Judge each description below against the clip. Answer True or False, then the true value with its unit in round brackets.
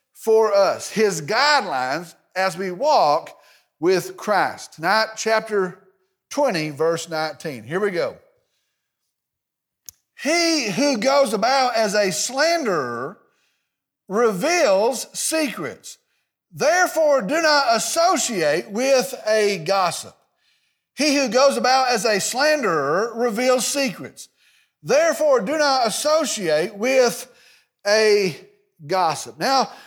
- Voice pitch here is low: False (240 Hz)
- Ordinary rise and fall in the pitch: False (6.2 semitones)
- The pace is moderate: False (100 wpm)